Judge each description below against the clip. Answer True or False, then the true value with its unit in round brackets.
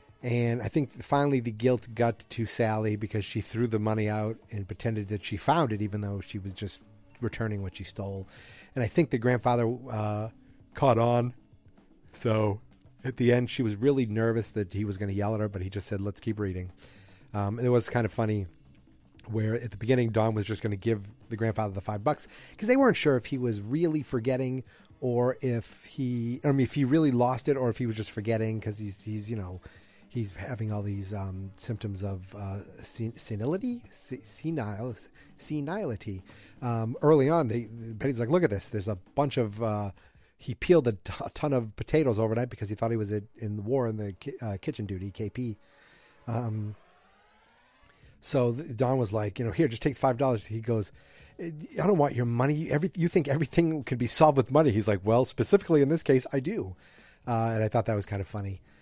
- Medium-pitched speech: False (115 Hz)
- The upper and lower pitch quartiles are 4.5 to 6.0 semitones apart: False (3.7 semitones)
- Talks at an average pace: False (215 wpm)